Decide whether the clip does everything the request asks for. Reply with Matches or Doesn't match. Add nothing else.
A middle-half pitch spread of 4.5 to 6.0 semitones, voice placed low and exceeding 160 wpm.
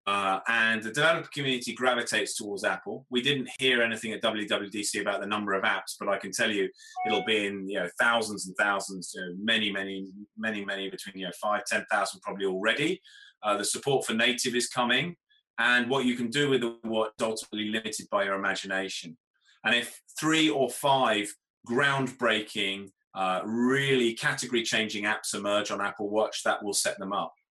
Doesn't match